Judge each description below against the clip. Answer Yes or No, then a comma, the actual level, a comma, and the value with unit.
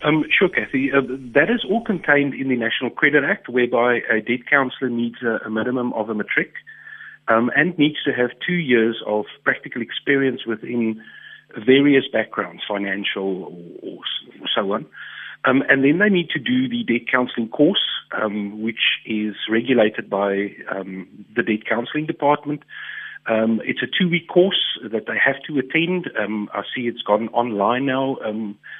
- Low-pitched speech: Yes, low, 125 Hz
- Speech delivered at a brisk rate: No, average, 170 wpm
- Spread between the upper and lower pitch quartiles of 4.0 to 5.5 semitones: Yes, average, 4.7 semitones